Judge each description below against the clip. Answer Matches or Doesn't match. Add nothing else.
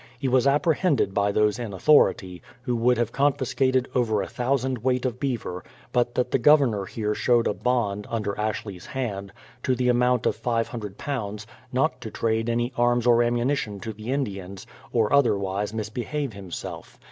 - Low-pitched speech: Matches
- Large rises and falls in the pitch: Doesn't match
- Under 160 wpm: Doesn't match